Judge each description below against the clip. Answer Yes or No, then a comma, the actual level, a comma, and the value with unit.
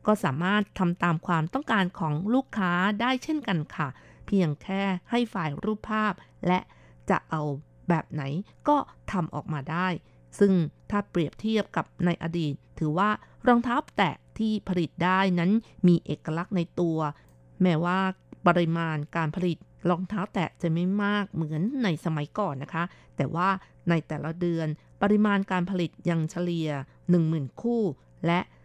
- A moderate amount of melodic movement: Yes, average, 4.0 semitones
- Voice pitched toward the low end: No, medium, 175 Hz